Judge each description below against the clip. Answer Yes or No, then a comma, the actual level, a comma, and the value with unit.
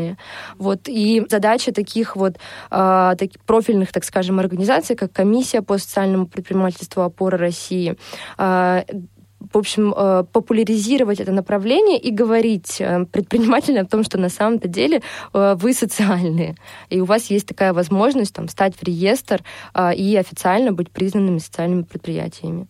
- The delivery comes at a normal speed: Yes, average, 130 wpm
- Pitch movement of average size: Yes, average, 3.1 semitones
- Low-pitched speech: No, high, 195 Hz